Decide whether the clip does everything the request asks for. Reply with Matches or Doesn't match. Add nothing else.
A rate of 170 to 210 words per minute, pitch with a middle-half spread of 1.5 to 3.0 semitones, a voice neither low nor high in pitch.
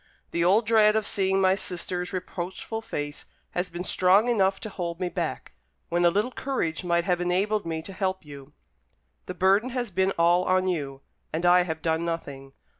Matches